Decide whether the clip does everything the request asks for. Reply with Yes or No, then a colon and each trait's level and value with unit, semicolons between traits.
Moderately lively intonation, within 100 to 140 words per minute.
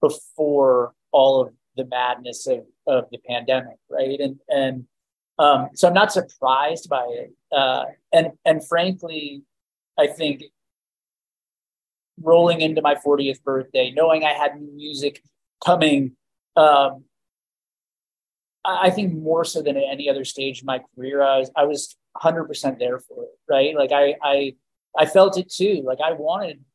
No: average, 3.4 semitones; average, 150 wpm